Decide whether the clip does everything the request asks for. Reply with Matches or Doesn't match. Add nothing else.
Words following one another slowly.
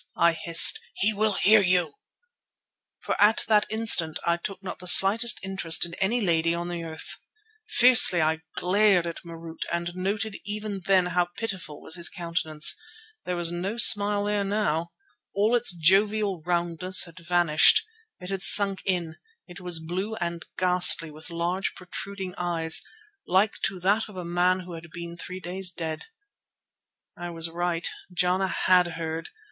Doesn't match